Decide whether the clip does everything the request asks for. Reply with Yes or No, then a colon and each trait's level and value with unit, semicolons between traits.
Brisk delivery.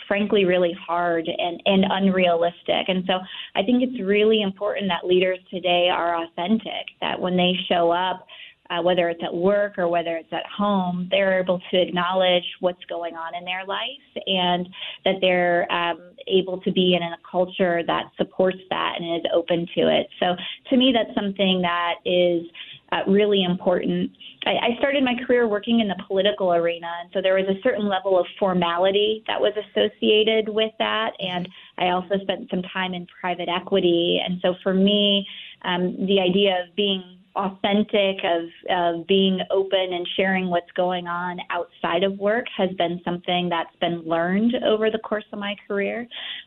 No: average, 180 wpm